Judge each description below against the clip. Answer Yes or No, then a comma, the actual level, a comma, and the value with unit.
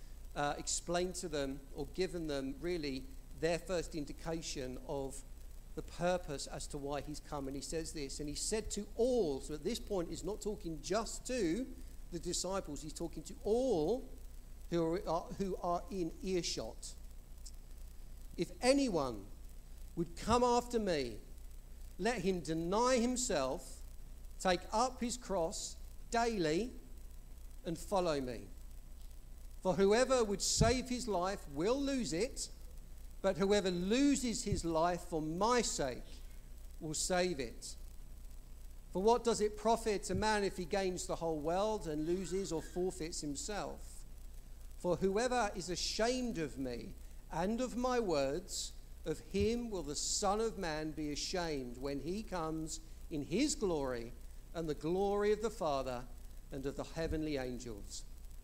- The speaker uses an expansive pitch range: Yes, wide, 8.8 semitones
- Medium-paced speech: Yes, average, 145 wpm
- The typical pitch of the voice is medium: Yes, medium, 160 Hz